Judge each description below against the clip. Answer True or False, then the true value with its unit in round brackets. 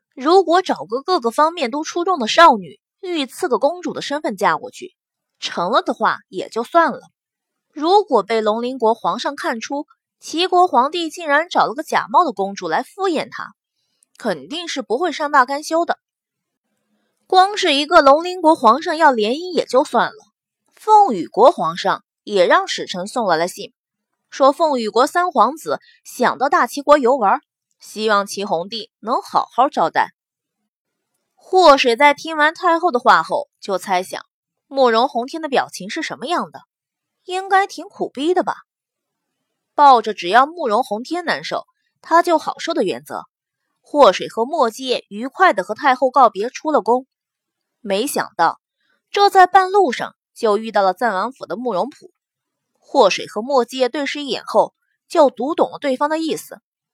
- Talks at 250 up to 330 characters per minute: False (240 characters per minute)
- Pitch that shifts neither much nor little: False (6.6 semitones)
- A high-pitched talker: True (295 Hz)